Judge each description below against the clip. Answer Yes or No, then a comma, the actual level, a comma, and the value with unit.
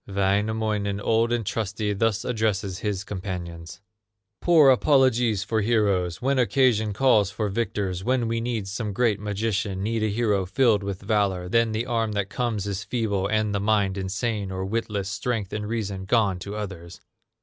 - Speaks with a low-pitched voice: Yes, low, 105 Hz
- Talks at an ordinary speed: Yes, average, 165 wpm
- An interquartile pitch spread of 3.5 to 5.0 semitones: No, narrow, 2.6 semitones